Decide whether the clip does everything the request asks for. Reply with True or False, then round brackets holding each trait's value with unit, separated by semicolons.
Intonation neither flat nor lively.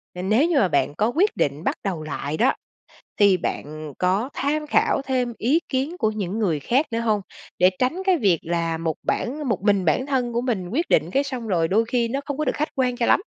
False (6.9 semitones)